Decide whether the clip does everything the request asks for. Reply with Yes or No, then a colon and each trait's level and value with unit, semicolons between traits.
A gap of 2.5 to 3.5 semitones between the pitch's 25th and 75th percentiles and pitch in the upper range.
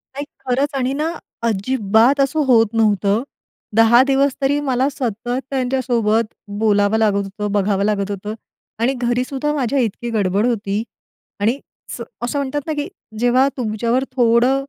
No: average, 4.1 semitones; high, 240 Hz